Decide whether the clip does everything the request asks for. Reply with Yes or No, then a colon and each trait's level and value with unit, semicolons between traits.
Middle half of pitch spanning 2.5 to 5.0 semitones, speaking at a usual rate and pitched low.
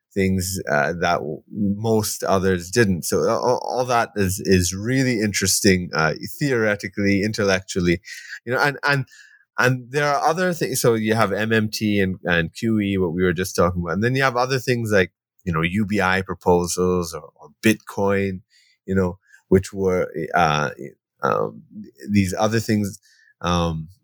Yes: average, 3.2 semitones; average, 155 wpm; low, 100 Hz